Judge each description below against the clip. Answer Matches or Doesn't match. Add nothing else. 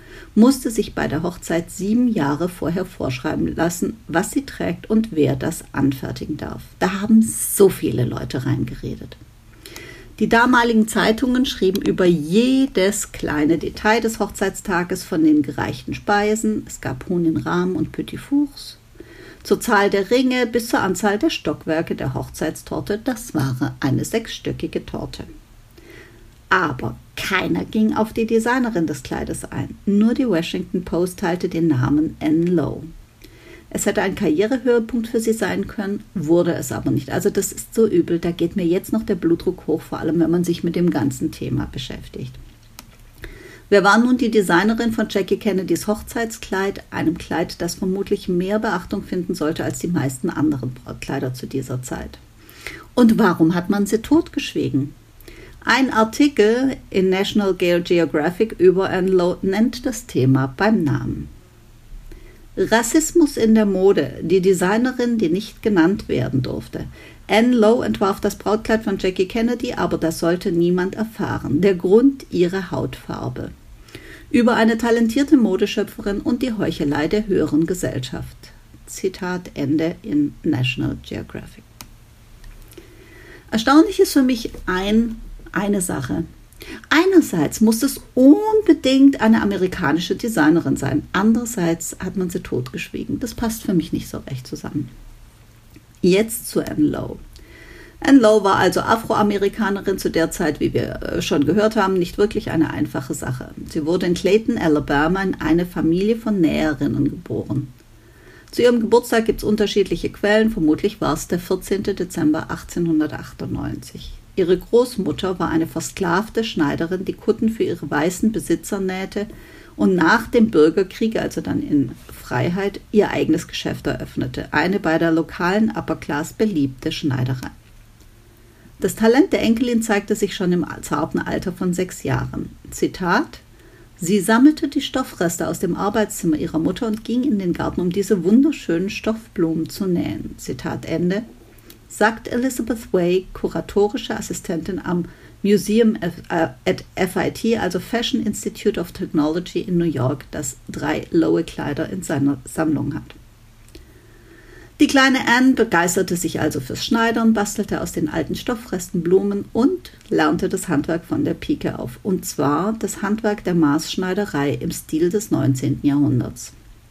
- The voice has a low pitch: Doesn't match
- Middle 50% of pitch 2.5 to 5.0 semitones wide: Doesn't match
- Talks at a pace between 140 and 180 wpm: Matches